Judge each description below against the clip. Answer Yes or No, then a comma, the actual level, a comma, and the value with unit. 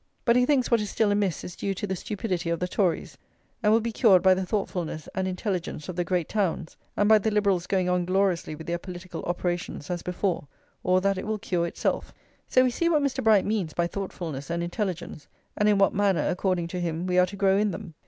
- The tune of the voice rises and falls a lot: No, average, 3.0 semitones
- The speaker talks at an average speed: No, fast, 235 wpm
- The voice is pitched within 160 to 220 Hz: Yes, medium, 185 Hz